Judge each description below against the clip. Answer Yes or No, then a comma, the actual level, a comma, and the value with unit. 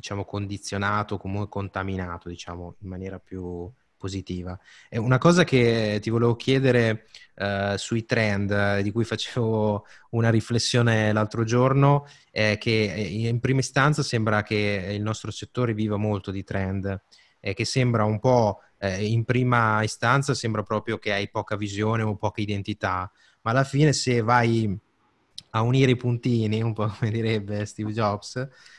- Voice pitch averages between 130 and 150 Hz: No, low, 110 Hz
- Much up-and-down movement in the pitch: No, average, 2.7 semitones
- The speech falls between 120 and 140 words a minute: No, average, 150 wpm